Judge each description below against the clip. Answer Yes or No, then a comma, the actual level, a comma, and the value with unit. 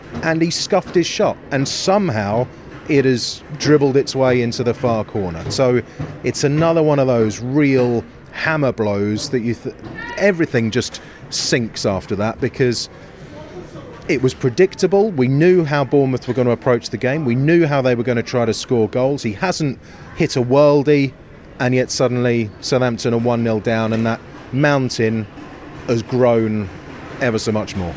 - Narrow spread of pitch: No, average, 3.7 semitones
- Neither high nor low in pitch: No, low, 125 Hz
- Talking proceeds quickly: No, average, 170 wpm